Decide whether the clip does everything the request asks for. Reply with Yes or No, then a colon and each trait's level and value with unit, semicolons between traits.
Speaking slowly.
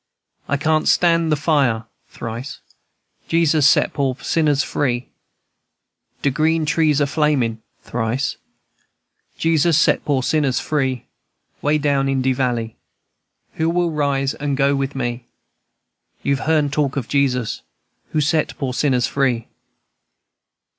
Yes: slow, 125 wpm